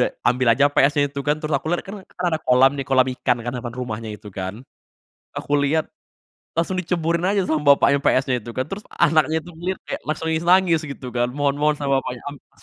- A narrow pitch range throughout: No, average, 4.1 semitones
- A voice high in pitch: No, medium, 145 Hz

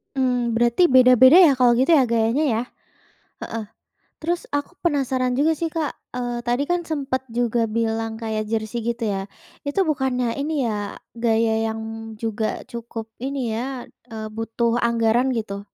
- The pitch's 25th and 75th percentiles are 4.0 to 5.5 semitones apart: No, average, 2.9 semitones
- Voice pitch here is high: Yes, high, 240 Hz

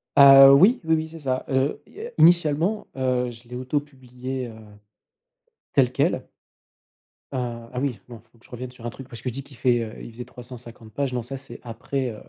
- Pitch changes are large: No, narrow, 2.5 semitones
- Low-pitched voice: Yes, low, 130 Hz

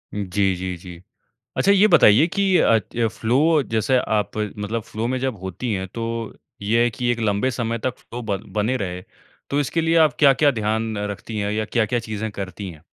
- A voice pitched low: Yes, low, 110 Hz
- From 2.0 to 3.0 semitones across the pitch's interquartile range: No, average, 3.7 semitones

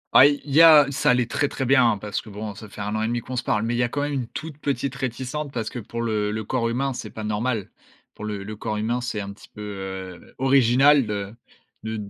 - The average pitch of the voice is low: Yes, low, 115 Hz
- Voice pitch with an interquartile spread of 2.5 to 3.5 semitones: No, average, 4.0 semitones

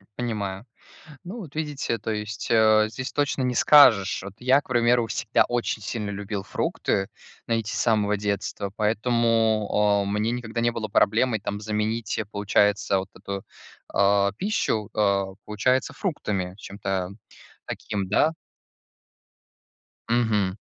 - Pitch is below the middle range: Yes, low, 110 Hz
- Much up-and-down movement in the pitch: No, average, 2.8 semitones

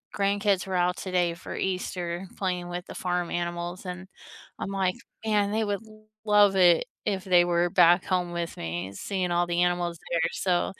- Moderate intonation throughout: No, narrow, 1.7 semitones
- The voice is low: No, medium, 180 Hz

